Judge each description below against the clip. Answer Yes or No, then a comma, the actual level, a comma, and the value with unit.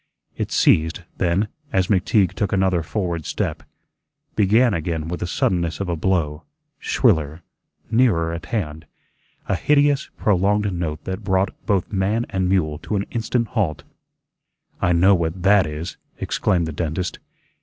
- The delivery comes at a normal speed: Yes, average, 145 wpm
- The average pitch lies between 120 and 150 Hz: No, very low, 90 Hz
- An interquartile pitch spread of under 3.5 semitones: No, average, 3.8 semitones